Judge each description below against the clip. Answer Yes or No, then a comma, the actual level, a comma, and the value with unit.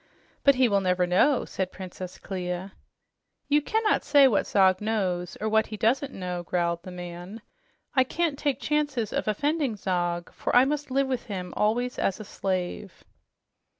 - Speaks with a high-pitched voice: Yes, high, 210 Hz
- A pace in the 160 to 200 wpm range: Yes, average, 170 wpm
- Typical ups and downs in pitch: No, wide, 6.5 semitones